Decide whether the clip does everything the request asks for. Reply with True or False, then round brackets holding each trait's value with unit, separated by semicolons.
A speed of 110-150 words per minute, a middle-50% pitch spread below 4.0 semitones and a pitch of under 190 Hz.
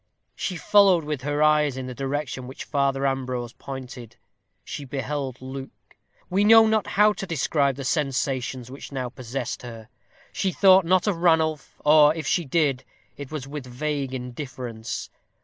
False (160 wpm; 3.4 semitones; 140 Hz)